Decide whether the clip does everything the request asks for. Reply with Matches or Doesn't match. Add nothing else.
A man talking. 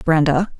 Doesn't match